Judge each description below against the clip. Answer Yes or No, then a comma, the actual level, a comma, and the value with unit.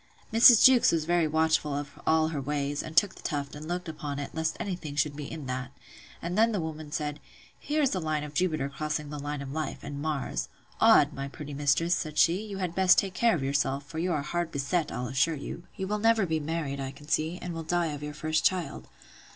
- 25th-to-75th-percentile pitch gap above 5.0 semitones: No, average, 3.2 semitones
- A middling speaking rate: No, fast, 240 wpm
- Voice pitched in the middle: Yes, medium, 155 Hz